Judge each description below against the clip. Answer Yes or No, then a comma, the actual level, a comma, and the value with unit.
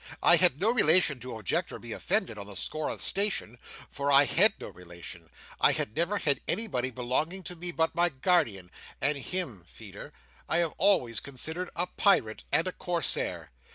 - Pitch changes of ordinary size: No, wide, 6.7 semitones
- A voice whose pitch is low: No, medium, 155 Hz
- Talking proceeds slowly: No, average, 190 wpm